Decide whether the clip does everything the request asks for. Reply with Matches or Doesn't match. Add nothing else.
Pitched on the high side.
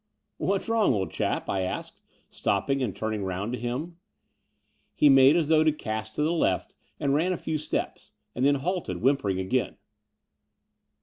Doesn't match